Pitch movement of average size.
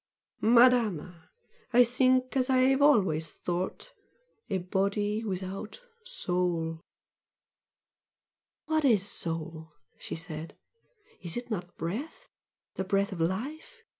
No: wide, 6.5 semitones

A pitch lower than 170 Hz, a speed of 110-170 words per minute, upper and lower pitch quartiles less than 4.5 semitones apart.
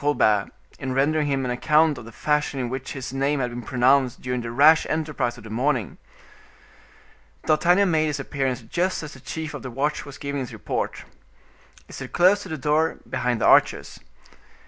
No: medium, 140 Hz; average, 190 wpm; average, 3.5 semitones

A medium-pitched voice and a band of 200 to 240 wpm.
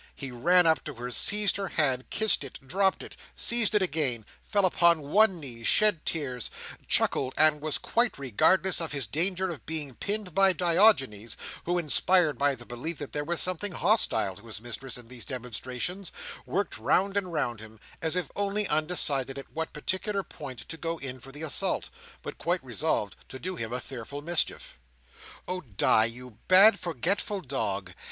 No: medium, 155 Hz; average, 180 wpm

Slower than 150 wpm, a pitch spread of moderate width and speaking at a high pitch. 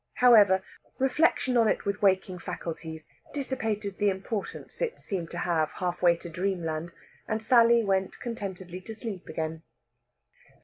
Yes: average, 140 wpm; average, 4.3 semitones; high, 195 Hz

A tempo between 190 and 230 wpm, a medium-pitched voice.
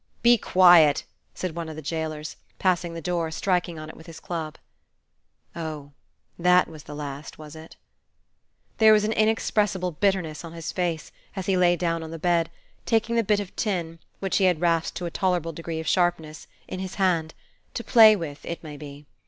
Yes: average, 195 wpm; medium, 170 Hz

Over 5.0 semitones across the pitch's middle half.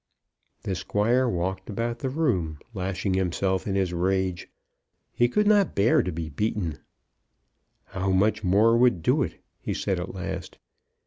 No: average, 4.0 semitones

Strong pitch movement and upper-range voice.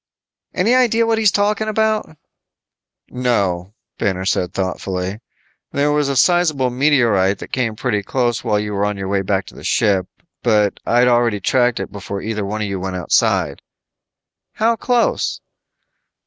No: wide, 7.0 semitones; low, 115 Hz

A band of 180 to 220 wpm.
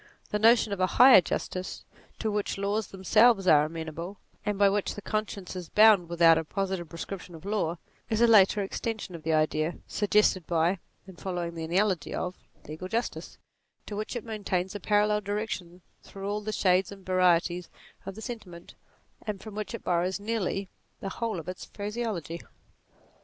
Yes: average, 185 wpm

